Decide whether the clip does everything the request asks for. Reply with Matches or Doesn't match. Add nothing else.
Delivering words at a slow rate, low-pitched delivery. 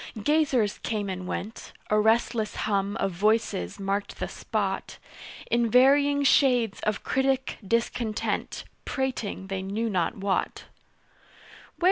Doesn't match